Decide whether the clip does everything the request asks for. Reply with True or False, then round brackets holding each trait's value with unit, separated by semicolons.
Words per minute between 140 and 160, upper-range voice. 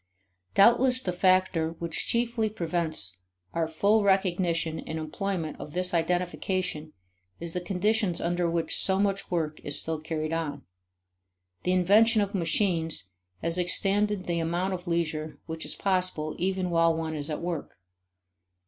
False (145 wpm; 175 Hz)